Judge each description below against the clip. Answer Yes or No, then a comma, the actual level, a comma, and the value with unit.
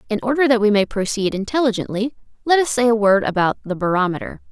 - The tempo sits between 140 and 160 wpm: No, average, 200 wpm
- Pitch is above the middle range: Yes, high, 220 Hz